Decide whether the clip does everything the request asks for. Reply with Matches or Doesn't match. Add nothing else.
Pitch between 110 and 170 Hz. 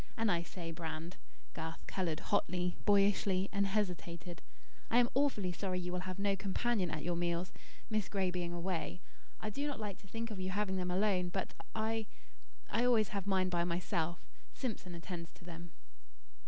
Doesn't match